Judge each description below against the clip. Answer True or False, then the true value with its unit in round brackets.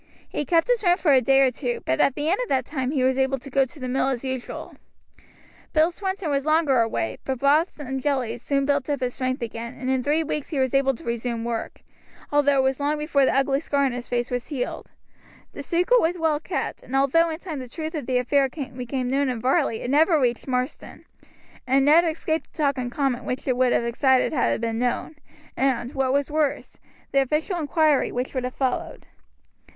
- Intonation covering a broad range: False (3.1 semitones)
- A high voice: True (270 Hz)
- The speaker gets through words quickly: True (230 wpm)